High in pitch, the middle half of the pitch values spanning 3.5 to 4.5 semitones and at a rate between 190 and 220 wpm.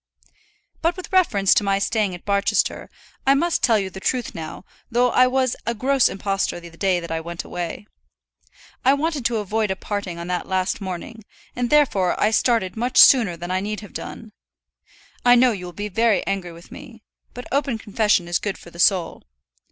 No: high, 210 Hz; average, 4.9 semitones; average, 200 wpm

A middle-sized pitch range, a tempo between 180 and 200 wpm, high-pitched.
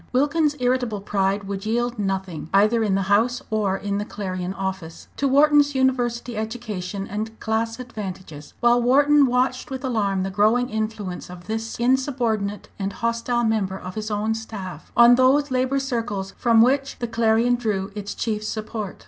No: average, 3.7 semitones; average, 165 wpm; high, 220 Hz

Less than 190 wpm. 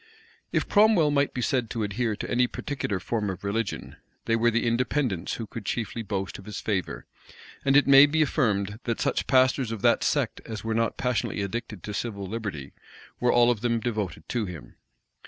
No: average, 195 wpm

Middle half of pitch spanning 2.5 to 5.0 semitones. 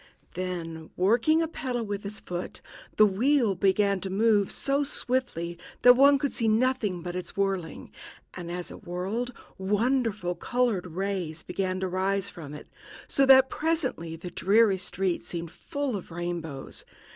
No: wide, 5.6 semitones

